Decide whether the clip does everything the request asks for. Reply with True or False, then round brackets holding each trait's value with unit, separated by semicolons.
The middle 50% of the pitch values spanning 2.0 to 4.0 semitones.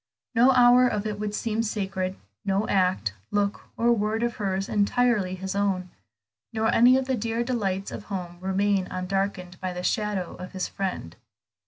True (3.2 semitones)